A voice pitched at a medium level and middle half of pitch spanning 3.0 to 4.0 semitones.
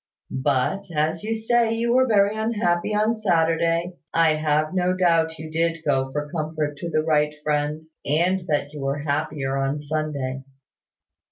Yes: medium, 160 Hz; average, 3.7 semitones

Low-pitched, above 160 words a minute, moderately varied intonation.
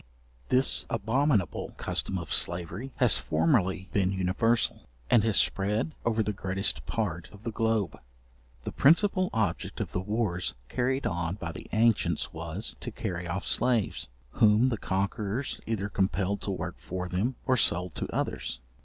No: low, 105 Hz; average, 155 wpm; average, 3.9 semitones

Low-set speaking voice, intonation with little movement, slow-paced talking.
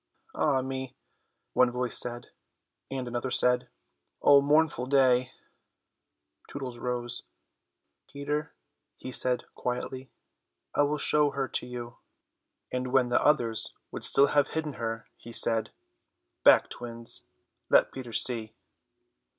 Yes: low, 125 Hz; narrow, 2.3 semitones; slow, 120 wpm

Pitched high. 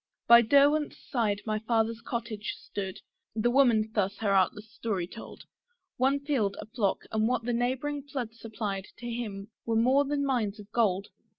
Yes: high, 225 Hz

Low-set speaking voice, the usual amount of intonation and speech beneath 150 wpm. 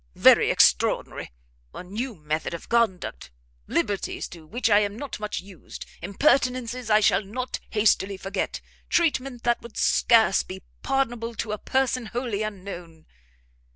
No: high, 215 Hz; average, 4.1 semitones; average, 140 wpm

